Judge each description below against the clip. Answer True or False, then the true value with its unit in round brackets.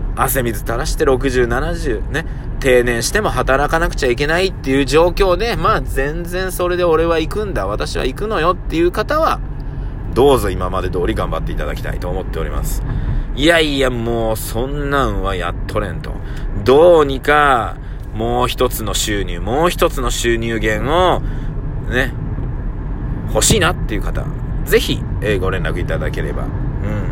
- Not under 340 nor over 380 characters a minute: False (305 characters per minute)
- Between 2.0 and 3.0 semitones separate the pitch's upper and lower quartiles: False (5.1 semitones)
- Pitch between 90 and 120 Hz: False (130 Hz)